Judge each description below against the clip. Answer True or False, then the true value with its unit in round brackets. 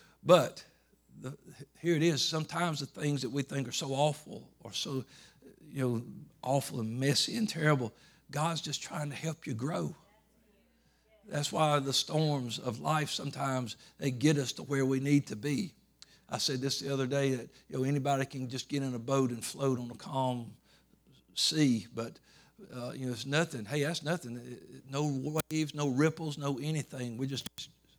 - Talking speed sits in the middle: True (180 wpm)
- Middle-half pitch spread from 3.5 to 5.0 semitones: False (2.7 semitones)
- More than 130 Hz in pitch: True (140 Hz)